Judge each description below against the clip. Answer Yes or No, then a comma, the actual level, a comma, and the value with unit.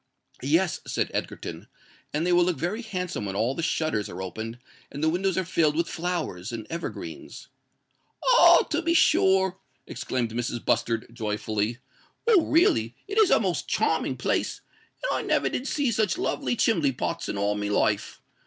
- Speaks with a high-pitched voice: No, medium, 165 Hz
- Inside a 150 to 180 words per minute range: Yes, average, 170 wpm